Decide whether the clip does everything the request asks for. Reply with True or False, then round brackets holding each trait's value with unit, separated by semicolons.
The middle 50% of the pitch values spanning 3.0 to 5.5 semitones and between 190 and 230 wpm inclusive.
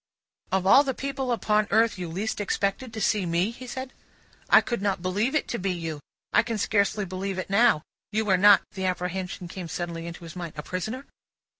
True (3.8 semitones; 205 wpm)